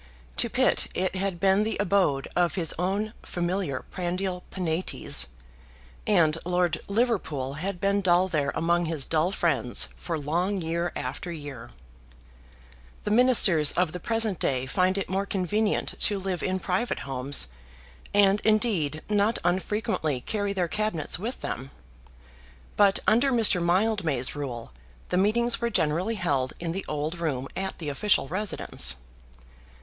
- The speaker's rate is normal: Yes, average, 145 wpm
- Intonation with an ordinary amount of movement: Yes, average, 4.4 semitones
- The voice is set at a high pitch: No, medium, 180 Hz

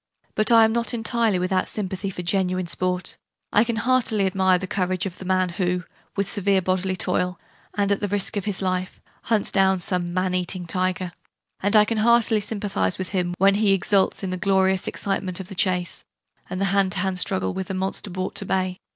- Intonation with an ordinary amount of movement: No, narrow, 1.7 semitones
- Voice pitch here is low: No, high, 190 Hz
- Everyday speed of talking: No, fast, 210 wpm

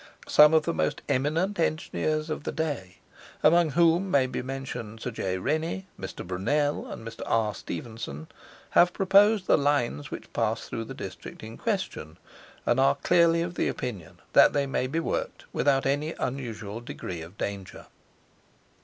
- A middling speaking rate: Yes, average, 160 wpm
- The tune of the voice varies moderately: No, wide, 6.7 semitones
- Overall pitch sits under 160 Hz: Yes, medium, 140 Hz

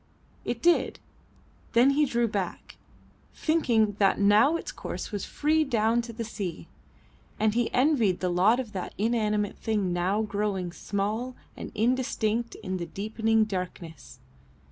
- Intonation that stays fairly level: No, average, 3.2 semitones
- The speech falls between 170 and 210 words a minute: No, average, 145 wpm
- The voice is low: No, high, 215 Hz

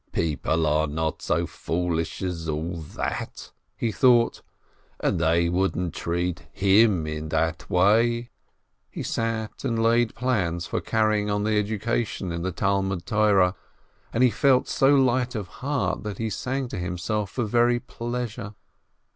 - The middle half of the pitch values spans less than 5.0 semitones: No, wide, 5.4 semitones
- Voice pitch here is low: Yes, low, 105 Hz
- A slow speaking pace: No, average, 150 wpm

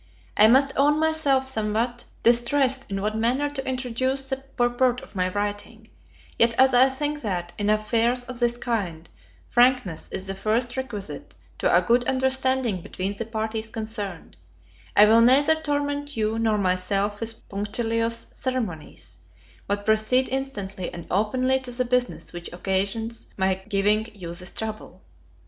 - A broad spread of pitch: No, average, 4.1 semitones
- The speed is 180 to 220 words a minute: No, average, 150 wpm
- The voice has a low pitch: No, high, 230 Hz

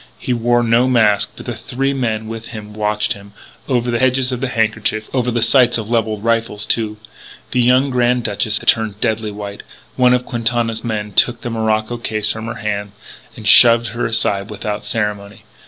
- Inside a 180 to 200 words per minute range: Yes, average, 190 wpm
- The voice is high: No, low, 115 Hz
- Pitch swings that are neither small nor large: No, narrow, 2.2 semitones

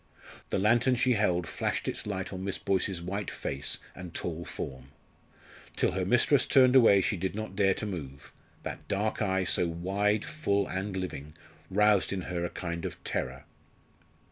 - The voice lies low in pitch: Yes, very low, 95 Hz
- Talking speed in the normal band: Yes, average, 170 wpm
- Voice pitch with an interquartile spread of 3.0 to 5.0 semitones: Yes, average, 3.3 semitones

